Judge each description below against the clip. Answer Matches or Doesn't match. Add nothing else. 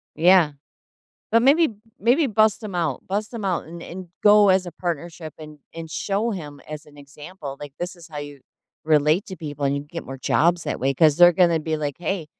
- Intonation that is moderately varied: Matches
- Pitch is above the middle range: Doesn't match